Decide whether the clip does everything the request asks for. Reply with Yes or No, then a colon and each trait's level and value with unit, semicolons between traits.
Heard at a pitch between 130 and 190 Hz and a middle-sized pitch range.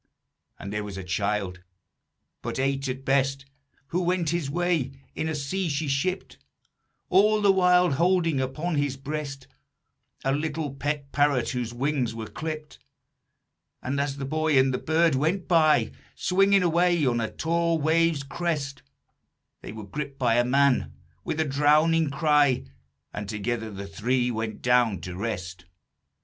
Yes: medium, 140 Hz; average, 4.7 semitones